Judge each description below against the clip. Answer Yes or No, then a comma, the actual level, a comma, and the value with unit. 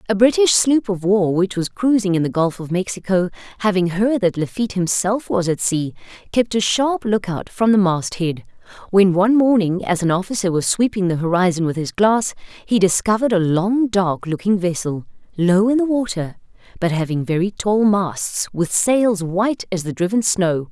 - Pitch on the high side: Yes, high, 195 Hz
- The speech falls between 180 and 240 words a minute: Yes, average, 190 wpm